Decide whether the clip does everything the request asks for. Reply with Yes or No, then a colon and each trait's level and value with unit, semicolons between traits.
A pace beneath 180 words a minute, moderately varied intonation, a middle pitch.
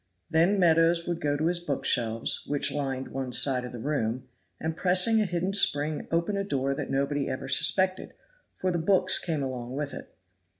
No: average, 195 wpm; average, 4.6 semitones; medium, 150 Hz